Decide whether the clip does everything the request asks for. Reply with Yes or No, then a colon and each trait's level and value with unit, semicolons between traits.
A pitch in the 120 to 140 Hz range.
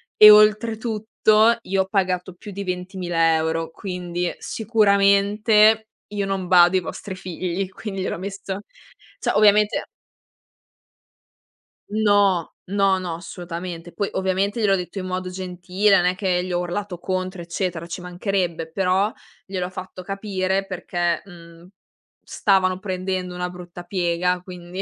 No: medium, 185 Hz